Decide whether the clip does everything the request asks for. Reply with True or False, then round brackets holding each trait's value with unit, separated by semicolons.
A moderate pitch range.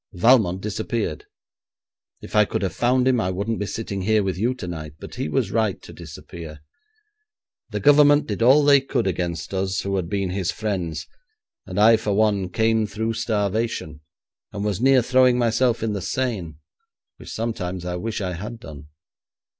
True (3.9 semitones)